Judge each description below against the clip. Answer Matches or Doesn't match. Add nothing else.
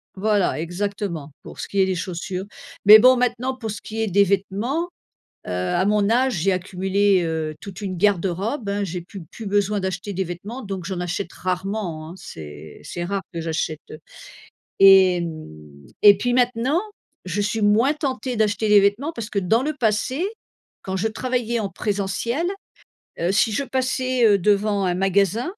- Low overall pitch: Doesn't match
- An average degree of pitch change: Matches